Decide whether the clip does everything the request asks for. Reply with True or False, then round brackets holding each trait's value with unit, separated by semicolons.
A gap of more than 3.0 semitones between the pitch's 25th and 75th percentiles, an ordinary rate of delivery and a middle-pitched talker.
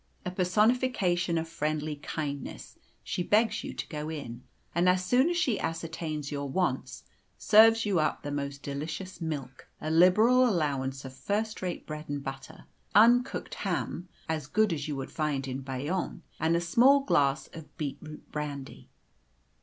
True (5.1 semitones; 160 wpm; 160 Hz)